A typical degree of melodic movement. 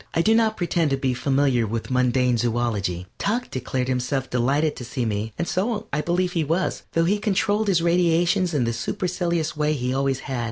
No: wide, 5.8 semitones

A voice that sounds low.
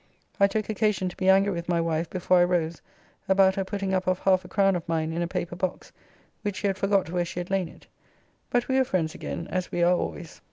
No: medium, 185 Hz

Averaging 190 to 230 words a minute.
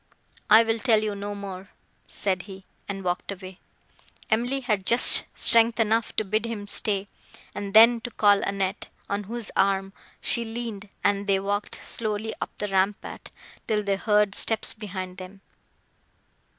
No: average, 155 wpm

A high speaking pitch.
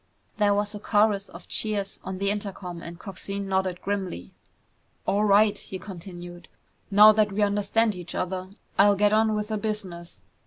Yes: high, 200 Hz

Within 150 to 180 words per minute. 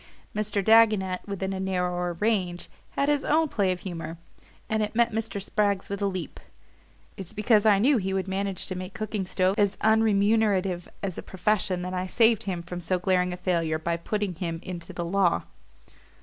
No: average, 190 wpm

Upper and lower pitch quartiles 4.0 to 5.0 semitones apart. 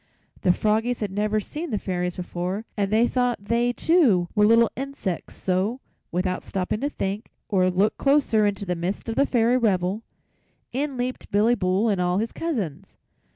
Yes: average, 4.6 semitones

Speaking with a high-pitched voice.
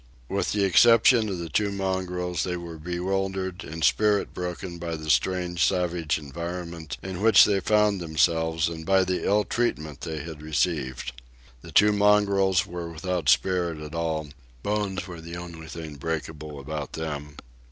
No: very low, 85 Hz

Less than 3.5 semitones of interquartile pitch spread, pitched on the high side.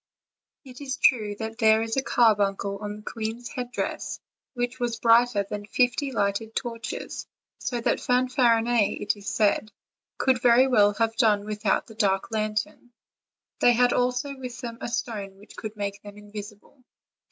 Yes: average, 2.9 semitones; high, 225 Hz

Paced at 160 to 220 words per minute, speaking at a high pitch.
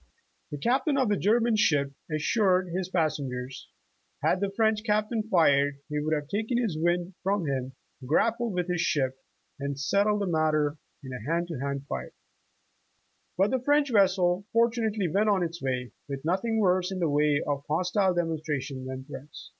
No: average, 175 wpm; medium, 175 Hz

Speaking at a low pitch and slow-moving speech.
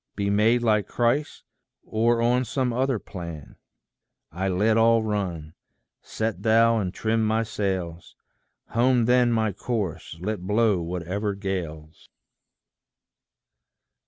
Yes: low, 110 Hz; slow, 115 wpm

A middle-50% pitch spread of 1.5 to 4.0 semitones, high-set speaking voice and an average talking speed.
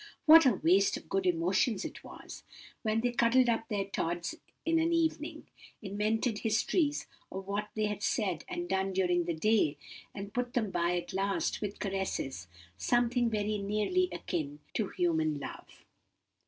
No: average, 4.5 semitones; high, 205 Hz; average, 160 wpm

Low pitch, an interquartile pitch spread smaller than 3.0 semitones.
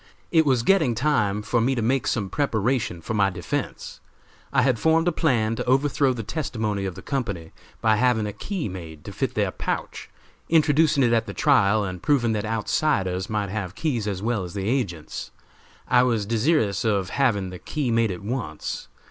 No: low, 115 Hz; average, 5.2 semitones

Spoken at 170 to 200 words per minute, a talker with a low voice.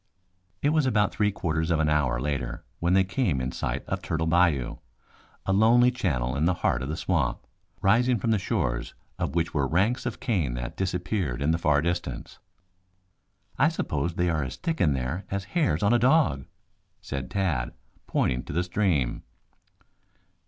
Yes: average, 180 wpm; very low, 85 Hz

